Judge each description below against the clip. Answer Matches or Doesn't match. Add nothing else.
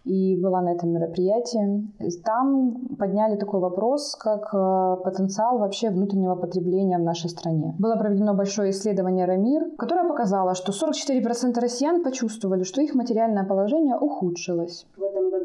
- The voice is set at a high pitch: Matches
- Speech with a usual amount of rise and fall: Matches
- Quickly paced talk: Doesn't match